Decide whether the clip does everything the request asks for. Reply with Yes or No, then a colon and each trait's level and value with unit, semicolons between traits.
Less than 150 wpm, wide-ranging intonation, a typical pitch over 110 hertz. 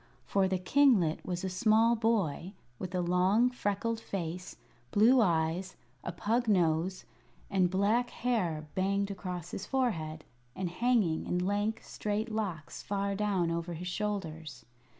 No: average, 140 wpm; average, 3.8 semitones; high, 190 Hz